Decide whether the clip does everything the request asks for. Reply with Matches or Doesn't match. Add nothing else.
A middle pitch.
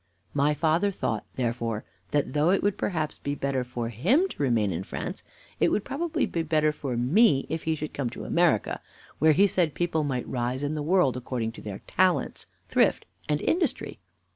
Matches